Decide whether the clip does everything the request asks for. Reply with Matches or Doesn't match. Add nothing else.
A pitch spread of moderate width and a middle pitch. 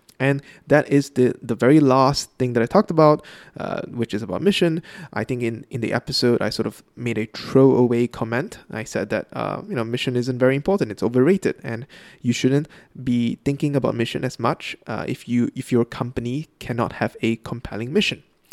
Doesn't match